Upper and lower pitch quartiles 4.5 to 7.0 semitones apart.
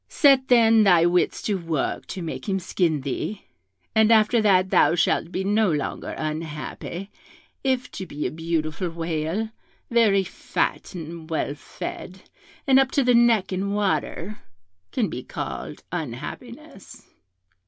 Yes: average, 5.1 semitones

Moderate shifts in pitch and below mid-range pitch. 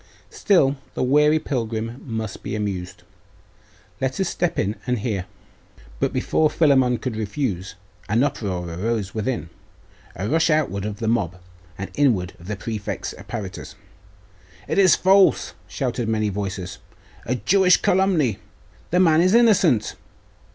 No: wide, 7.1 semitones; low, 115 Hz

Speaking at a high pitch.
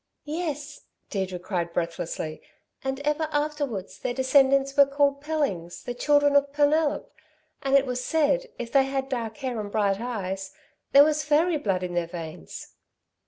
Yes: very high, 270 Hz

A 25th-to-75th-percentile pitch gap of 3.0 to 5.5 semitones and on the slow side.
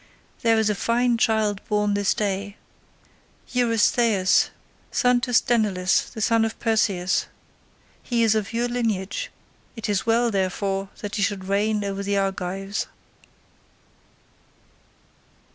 No: narrow, 2.6 semitones; slow, 125 wpm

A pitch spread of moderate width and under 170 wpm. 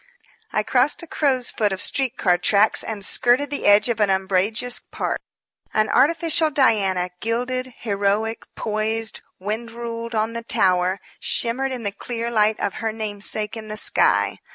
Yes: average, 3.0 semitones; average, 160 wpm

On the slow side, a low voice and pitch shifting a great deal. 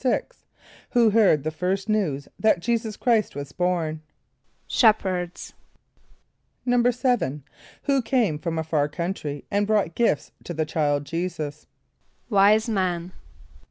No: slow, 125 wpm; medium, 180 Hz; wide, 5.7 semitones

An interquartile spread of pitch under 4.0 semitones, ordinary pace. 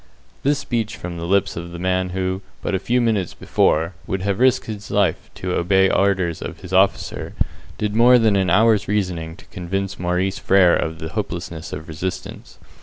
Yes: average, 2.9 semitones; average, 185 wpm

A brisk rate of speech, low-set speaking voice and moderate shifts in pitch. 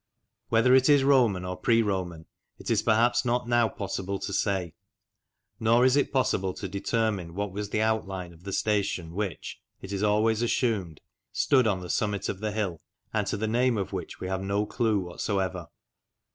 No: average, 185 wpm; low, 105 Hz; average, 3.3 semitones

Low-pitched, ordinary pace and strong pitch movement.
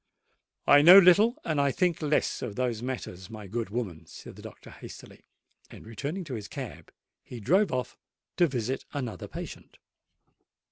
Yes: low, 130 Hz; average, 155 wpm; wide, 6.8 semitones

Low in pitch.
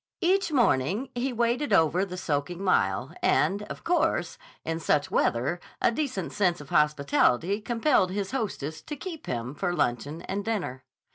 No: high, 190 Hz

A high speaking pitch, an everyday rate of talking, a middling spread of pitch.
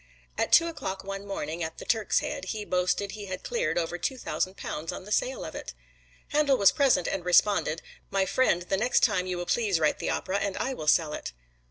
No: high, 195 Hz; fast, 225 wpm; average, 4.5 semitones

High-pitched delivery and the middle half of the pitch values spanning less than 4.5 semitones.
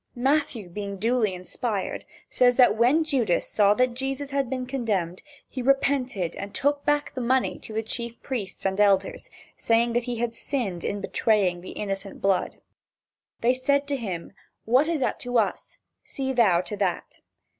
No: high, 235 Hz; average, 4.8 semitones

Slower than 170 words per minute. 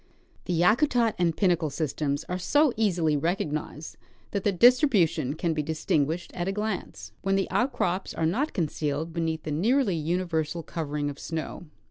Yes: average, 155 wpm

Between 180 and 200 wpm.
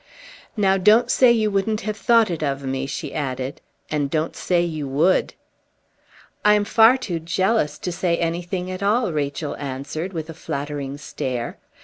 No: average, 165 wpm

